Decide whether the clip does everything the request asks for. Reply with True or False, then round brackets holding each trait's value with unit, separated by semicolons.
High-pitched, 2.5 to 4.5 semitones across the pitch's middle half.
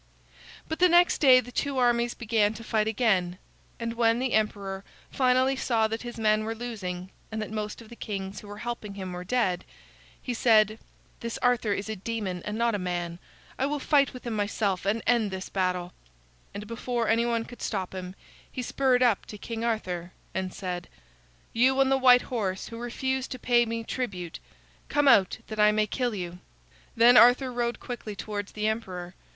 True (225 Hz; 3.5 semitones)